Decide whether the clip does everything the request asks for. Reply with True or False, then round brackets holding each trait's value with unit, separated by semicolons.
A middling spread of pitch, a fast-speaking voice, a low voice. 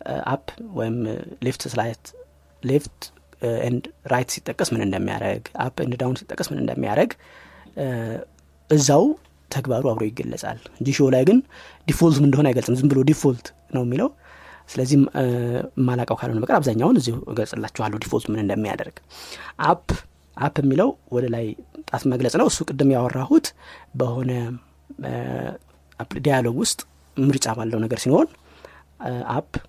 True (3.7 semitones; 120 wpm; 125 Hz)